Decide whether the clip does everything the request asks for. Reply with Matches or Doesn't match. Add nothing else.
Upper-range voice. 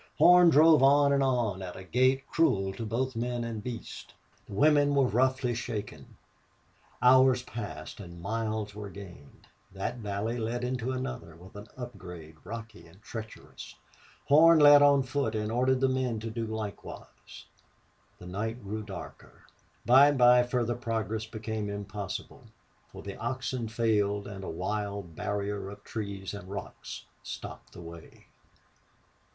Doesn't match